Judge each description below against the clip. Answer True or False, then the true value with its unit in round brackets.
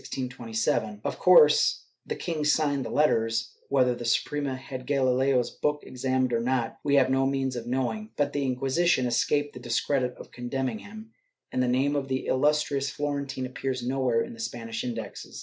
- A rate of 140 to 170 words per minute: False (180 wpm)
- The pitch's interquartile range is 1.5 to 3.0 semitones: True (2.6 semitones)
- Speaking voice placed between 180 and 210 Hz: False (130 Hz)